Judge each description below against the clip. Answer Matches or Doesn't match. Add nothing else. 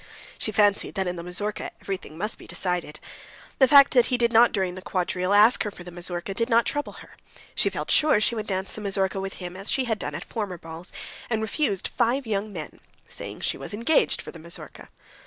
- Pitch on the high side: Matches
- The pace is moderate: Doesn't match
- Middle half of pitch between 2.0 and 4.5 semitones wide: Matches